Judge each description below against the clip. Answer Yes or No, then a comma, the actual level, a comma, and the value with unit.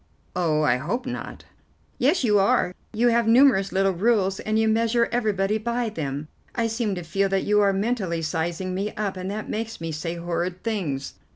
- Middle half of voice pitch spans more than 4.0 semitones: Yes, average, 4.6 semitones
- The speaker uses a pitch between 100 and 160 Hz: No, high, 195 Hz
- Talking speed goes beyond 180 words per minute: Yes, average, 190 wpm